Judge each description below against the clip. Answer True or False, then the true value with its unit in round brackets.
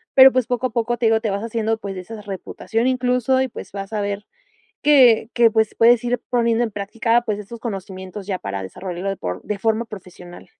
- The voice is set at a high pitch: True (220 Hz)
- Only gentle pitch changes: False (3.3 semitones)